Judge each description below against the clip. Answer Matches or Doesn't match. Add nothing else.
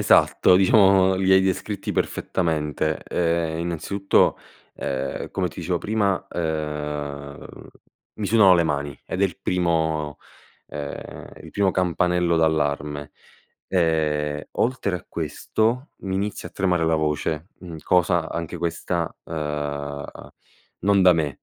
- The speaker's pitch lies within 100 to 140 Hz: Doesn't match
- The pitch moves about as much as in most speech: Matches